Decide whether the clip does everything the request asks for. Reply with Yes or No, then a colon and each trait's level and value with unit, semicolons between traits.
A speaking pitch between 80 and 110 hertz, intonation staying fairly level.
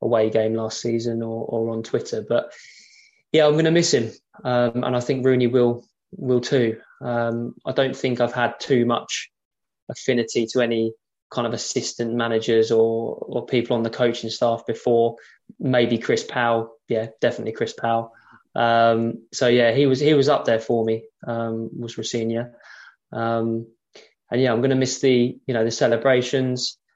No: low, 120 Hz; narrow, 1.9 semitones